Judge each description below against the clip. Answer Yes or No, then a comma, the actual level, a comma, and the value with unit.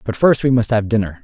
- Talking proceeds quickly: Yes, fast, 290 wpm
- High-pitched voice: No, low, 115 Hz